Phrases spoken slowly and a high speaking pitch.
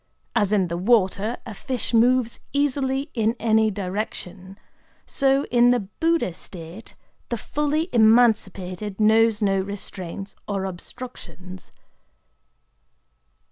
Yes: slow, 105 wpm; high, 220 Hz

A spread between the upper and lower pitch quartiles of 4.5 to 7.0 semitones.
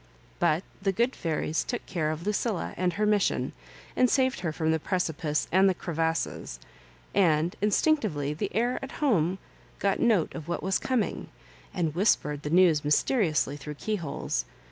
Yes: average, 5.3 semitones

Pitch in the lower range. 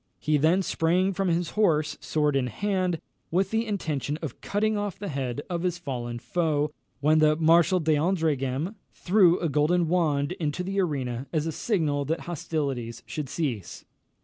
No: medium, 160 Hz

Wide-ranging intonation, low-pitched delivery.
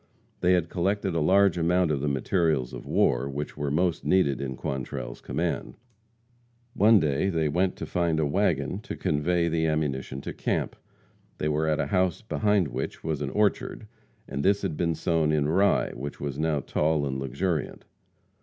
No: average, 4.2 semitones; very low, 80 Hz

